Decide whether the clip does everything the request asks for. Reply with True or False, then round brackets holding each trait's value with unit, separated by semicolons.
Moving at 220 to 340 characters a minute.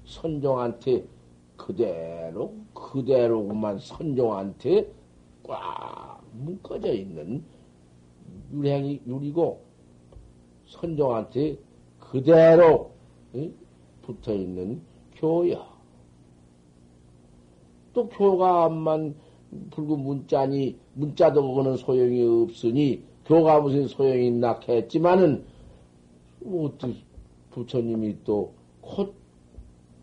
False (165 characters per minute)